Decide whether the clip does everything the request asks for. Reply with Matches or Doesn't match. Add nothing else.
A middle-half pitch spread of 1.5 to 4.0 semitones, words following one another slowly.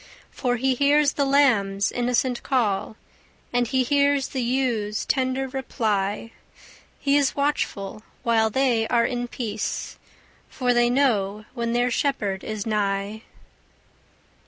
Matches